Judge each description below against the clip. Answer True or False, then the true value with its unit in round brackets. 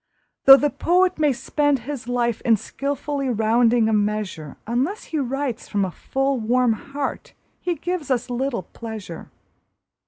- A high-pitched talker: True (250 Hz)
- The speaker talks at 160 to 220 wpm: False (150 wpm)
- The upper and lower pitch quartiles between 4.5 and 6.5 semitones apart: False (4.1 semitones)